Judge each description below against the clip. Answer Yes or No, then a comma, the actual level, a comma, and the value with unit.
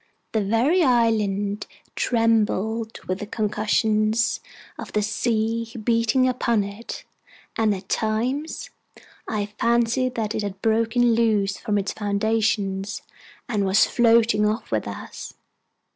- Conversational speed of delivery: No, slow, 120 wpm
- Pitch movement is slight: Yes, narrow, 2.0 semitones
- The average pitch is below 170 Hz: No, high, 220 Hz